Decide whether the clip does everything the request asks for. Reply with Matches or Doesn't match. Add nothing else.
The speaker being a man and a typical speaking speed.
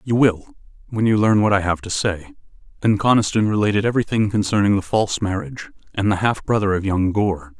Matches